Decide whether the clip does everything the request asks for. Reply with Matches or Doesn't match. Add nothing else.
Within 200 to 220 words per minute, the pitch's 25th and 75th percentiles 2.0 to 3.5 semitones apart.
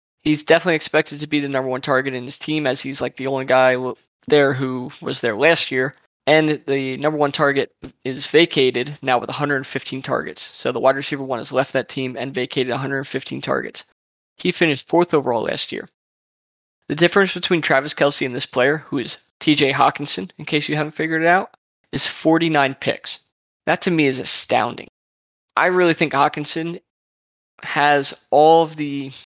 Doesn't match